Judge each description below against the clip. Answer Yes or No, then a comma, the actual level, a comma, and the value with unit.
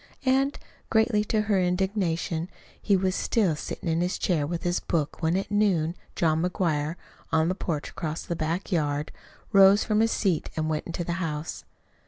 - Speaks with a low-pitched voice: No, medium, 175 Hz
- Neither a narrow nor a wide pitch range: Yes, average, 3.6 semitones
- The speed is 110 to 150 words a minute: No, average, 180 wpm